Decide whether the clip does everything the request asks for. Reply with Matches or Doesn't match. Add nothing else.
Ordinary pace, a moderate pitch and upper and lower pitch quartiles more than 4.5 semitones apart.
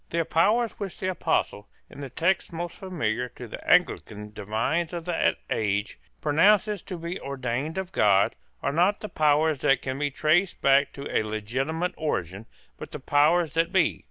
Matches